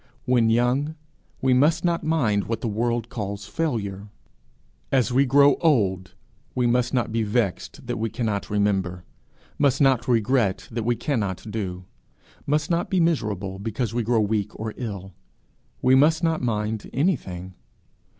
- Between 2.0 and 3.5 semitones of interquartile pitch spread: No, average, 4.7 semitones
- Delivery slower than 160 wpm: Yes, average, 150 wpm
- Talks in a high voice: No, low, 115 Hz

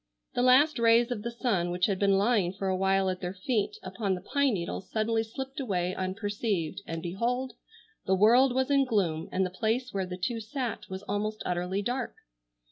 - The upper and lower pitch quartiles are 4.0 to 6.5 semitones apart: Yes, average, 4.6 semitones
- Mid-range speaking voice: No, high, 205 Hz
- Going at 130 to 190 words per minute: No, average, 200 wpm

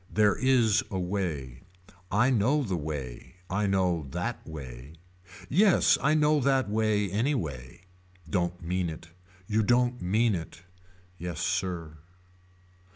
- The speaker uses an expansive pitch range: Yes, wide, 6.3 semitones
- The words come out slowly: Yes, slow, 125 wpm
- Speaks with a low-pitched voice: Yes, very low, 95 Hz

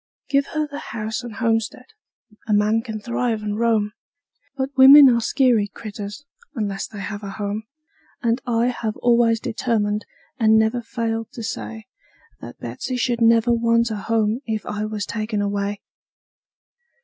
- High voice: Yes, high, 225 Hz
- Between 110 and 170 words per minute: Yes, average, 155 wpm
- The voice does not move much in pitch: Yes, narrow, 2.1 semitones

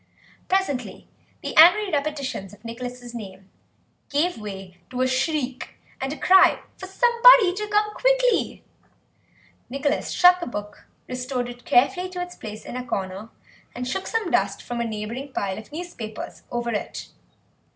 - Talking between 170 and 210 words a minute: No, average, 150 wpm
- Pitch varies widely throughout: Yes, wide, 7.9 semitones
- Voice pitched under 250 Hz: No, very high, 255 Hz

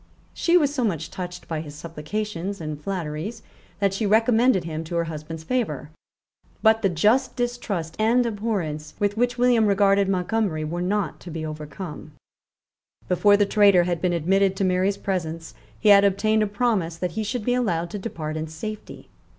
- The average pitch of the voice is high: Yes, high, 195 Hz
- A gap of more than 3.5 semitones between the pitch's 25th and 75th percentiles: Yes, average, 4.8 semitones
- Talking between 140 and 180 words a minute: Yes, average, 175 wpm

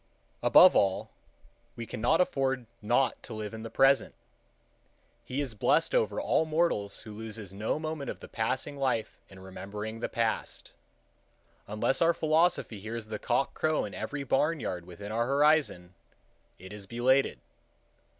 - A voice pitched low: Yes, low, 115 Hz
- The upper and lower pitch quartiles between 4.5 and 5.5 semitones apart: Yes, average, 4.8 semitones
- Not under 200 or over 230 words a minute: No, average, 150 wpm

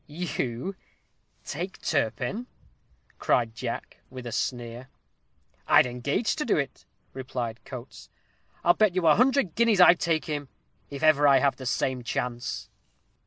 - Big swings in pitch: Yes, wide, 5.9 semitones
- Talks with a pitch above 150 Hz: No, medium, 140 Hz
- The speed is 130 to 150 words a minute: Yes, average, 140 wpm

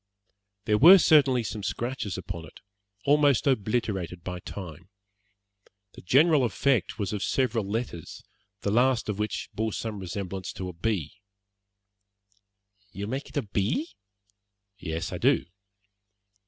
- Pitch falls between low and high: No, low, 105 Hz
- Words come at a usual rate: No, slow, 130 wpm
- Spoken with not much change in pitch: No, average, 5.2 semitones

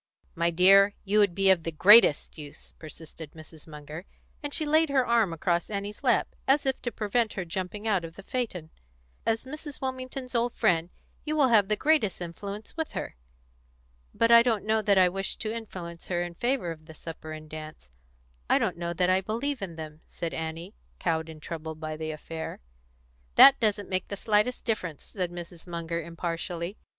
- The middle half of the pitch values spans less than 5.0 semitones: No, average, 5.3 semitones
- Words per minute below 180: No, average, 190 wpm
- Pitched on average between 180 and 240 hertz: Yes, medium, 185 Hz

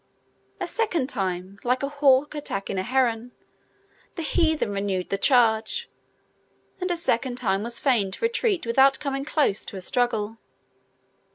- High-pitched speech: Yes, high, 245 Hz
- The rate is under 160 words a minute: Yes, average, 150 wpm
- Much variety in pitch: Yes, wide, 5.9 semitones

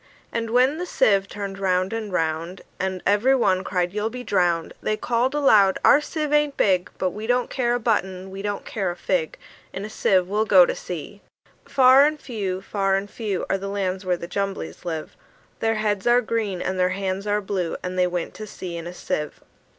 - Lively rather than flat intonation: No, average, 3.4 semitones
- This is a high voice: Yes, high, 195 Hz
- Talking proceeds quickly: Yes, fast, 215 wpm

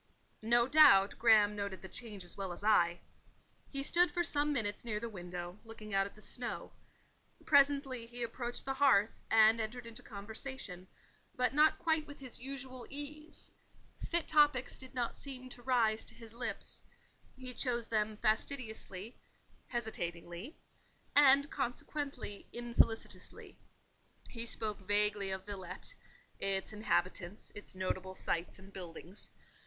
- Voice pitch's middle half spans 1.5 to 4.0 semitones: No, average, 4.6 semitones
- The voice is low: No, high, 225 Hz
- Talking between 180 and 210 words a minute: No, average, 140 wpm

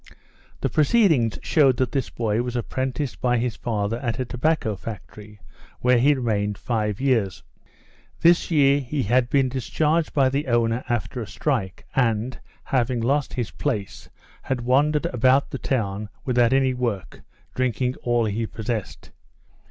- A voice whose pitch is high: No, low, 125 Hz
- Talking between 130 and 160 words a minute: Yes, average, 150 wpm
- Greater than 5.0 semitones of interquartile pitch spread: No, average, 3.0 semitones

